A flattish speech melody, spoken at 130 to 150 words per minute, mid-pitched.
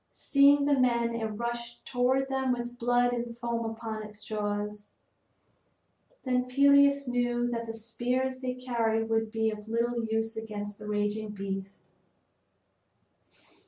No: narrow, 2.3 semitones; slow, 135 wpm; high, 235 Hz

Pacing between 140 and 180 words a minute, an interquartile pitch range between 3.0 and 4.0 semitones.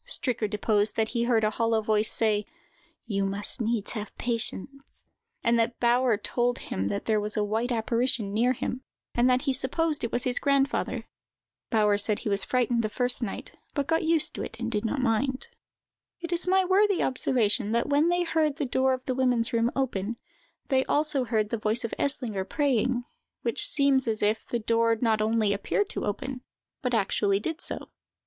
No: average, 195 wpm; average, 3.5 semitones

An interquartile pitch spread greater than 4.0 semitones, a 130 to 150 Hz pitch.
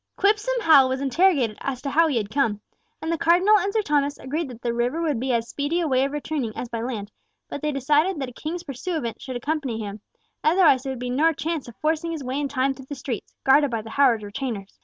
No: average, 4.6 semitones; very high, 275 Hz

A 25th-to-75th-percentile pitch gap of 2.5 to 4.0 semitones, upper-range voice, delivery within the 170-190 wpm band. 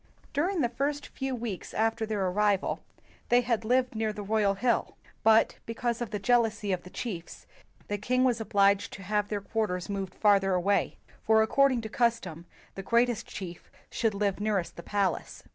Yes: average, 3.0 semitones; high, 215 Hz; average, 180 wpm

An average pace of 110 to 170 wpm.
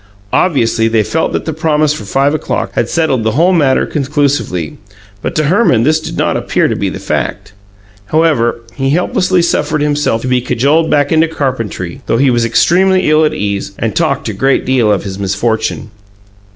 No: average, 190 wpm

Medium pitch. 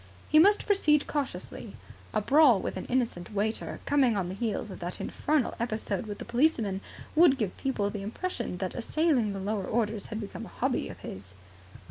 No: high, 225 Hz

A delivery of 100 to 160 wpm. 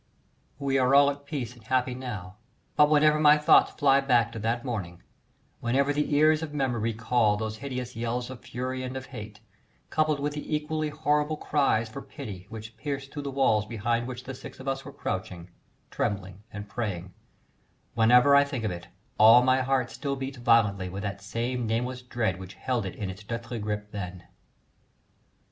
No: average, 185 wpm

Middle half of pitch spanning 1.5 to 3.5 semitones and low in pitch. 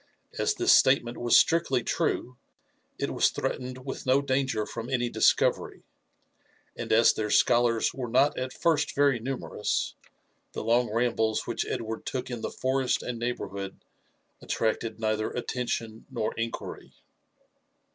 Yes: narrow, 2.5 semitones; low, 120 Hz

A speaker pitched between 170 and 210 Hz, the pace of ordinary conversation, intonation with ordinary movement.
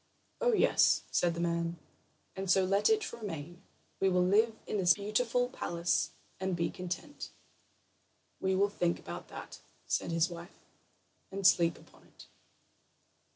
Yes: medium, 185 Hz; average, 145 wpm; average, 3.1 semitones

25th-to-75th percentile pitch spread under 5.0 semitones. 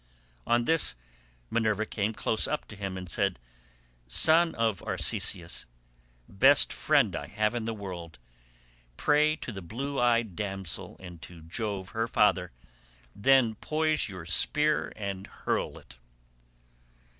No: wide, 5.4 semitones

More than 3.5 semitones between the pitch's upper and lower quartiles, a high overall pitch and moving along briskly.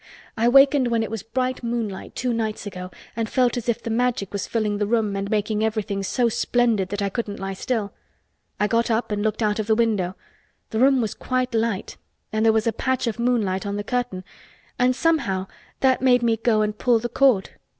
No: average, 2.8 semitones; high, 225 Hz; fast, 215 wpm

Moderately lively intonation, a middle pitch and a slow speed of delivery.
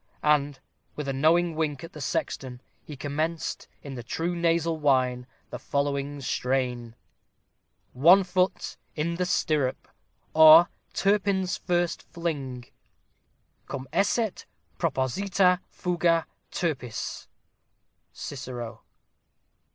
Yes: average, 4.5 semitones; medium, 155 Hz; slow, 100 wpm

